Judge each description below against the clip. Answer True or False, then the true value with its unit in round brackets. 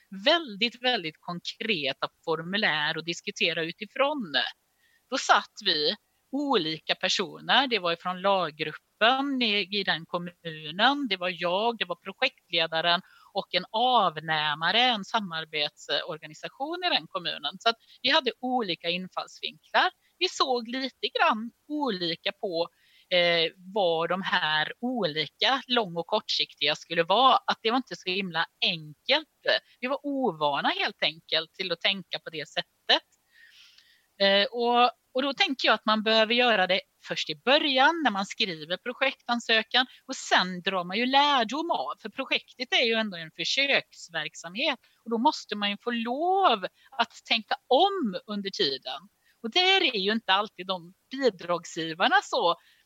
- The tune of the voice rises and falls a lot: True (7.1 semitones)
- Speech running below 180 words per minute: True (145 wpm)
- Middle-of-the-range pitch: False (215 Hz)